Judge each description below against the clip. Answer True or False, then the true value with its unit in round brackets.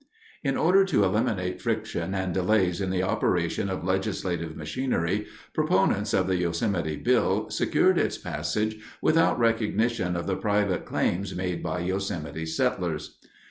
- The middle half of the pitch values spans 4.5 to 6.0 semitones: False (3.3 semitones)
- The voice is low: True (95 Hz)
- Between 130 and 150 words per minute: True (140 wpm)